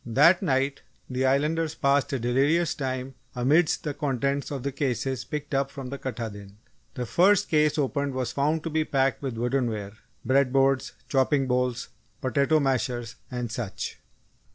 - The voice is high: No, low, 135 Hz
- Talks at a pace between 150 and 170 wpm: Yes, average, 155 wpm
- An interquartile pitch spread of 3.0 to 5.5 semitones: No, narrow, 2.5 semitones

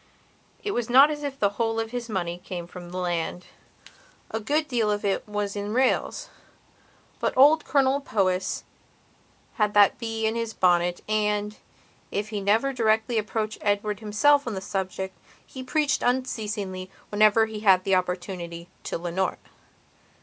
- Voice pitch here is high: Yes, high, 210 Hz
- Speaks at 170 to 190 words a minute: No, average, 155 wpm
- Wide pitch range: No, average, 3.6 semitones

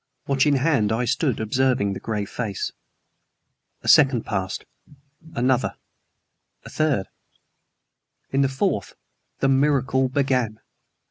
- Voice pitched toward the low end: Yes, low, 130 Hz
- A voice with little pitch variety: No, average, 3.7 semitones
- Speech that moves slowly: Yes, slow, 115 wpm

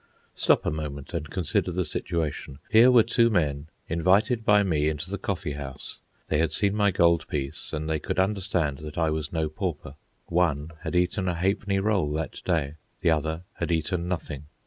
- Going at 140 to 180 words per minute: No, average, 190 wpm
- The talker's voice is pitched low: Yes, very low, 85 Hz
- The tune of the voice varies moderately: Yes, average, 3.9 semitones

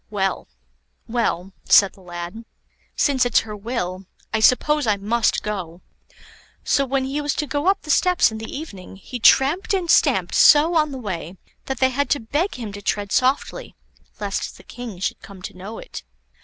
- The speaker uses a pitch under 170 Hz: No, high, 230 Hz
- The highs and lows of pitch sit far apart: Yes, wide, 6.2 semitones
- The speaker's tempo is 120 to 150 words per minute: No, average, 185 wpm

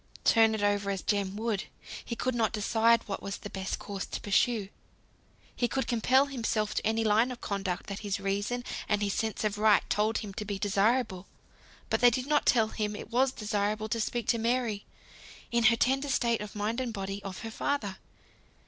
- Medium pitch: No, high, 215 Hz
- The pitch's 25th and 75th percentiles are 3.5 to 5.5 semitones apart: No, narrow, 2.6 semitones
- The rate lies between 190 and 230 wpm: Yes, average, 200 wpm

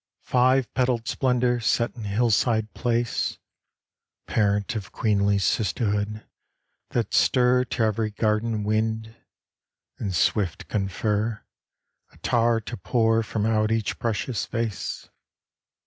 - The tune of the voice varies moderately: No, narrow, 2.1 semitones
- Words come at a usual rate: No, slow, 105 wpm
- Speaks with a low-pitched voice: Yes, low, 110 Hz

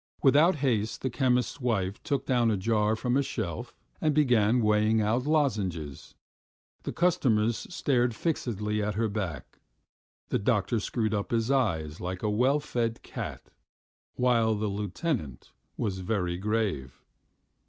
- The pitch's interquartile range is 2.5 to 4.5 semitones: Yes, average, 3.6 semitones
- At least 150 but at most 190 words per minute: No, average, 140 wpm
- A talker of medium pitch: No, low, 110 Hz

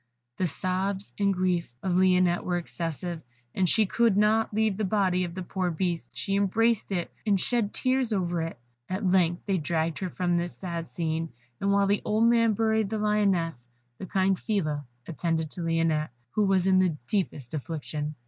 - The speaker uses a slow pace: No, average, 180 wpm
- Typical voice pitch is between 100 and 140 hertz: No, medium, 185 Hz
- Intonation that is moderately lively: Yes, average, 3.2 semitones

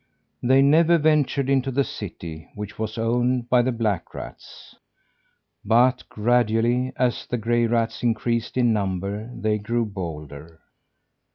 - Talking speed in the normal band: No, slow, 130 wpm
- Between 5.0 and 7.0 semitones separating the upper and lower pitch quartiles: No, average, 3.1 semitones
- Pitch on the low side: Yes, low, 115 Hz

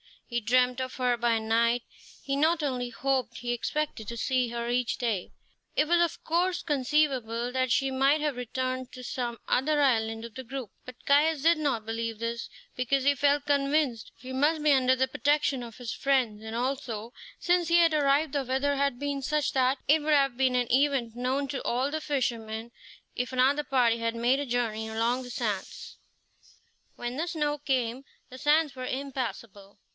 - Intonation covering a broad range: No, average, 3.2 semitones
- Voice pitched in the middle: No, very high, 260 Hz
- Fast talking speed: No, average, 190 wpm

